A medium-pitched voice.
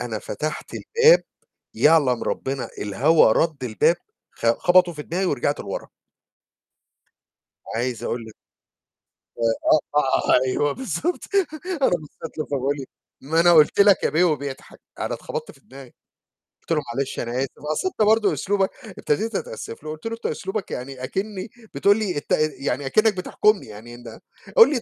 Yes: medium, 155 Hz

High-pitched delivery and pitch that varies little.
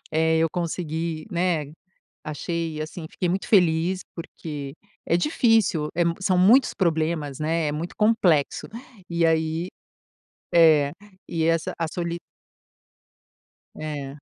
No: medium, 165 Hz; narrow, 2.1 semitones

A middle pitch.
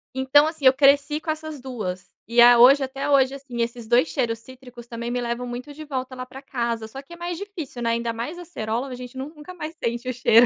No: very high, 255 Hz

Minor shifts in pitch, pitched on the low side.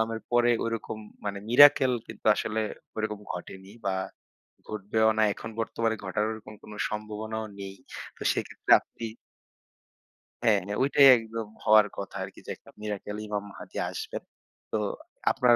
Yes: narrow, 1.6 semitones; low, 110 Hz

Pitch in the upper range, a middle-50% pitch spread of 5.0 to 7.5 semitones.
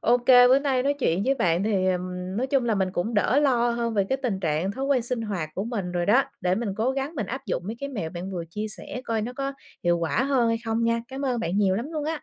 Yes: high, 230 Hz; wide, 5.6 semitones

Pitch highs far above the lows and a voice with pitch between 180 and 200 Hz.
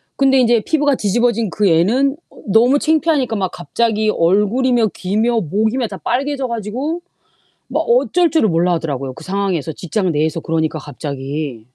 No: wide, 7.5 semitones; high, 215 Hz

